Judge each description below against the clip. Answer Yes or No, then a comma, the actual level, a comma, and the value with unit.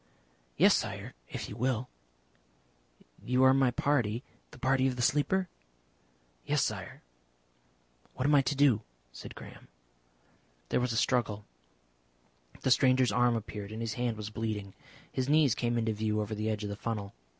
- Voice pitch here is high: No, low, 120 Hz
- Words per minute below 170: Yes, average, 160 wpm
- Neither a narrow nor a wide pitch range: Yes, average, 3.4 semitones